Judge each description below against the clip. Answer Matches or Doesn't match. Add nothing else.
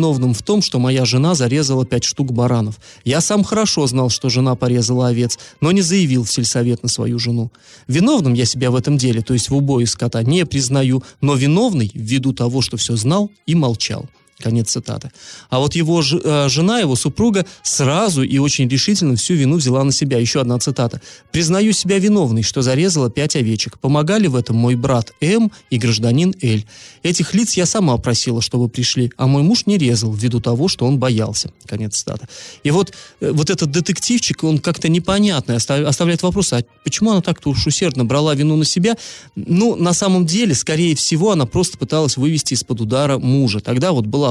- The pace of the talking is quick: Matches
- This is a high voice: Doesn't match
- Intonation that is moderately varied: Doesn't match